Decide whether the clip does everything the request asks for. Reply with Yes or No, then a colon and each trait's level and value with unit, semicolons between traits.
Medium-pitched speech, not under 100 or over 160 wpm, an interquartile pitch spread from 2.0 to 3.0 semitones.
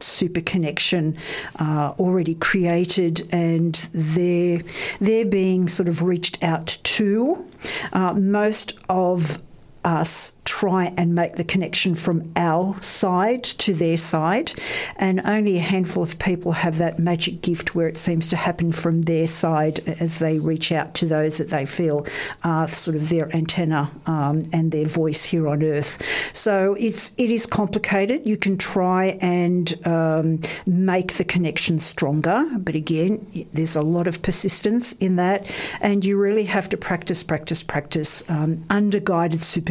Yes: medium, 175 Hz; average, 155 wpm; average, 2.7 semitones